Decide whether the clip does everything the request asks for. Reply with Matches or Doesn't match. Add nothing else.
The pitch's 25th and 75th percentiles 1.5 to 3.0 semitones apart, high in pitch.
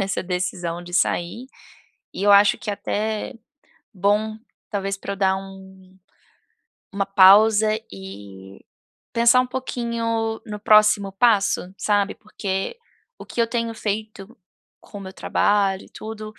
Matches